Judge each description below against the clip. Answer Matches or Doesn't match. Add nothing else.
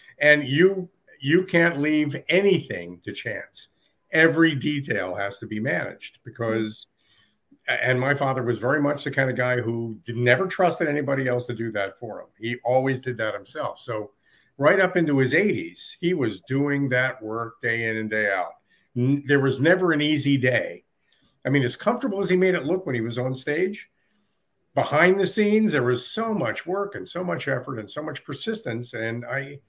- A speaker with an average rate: Matches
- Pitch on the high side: Doesn't match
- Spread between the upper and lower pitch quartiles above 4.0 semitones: Matches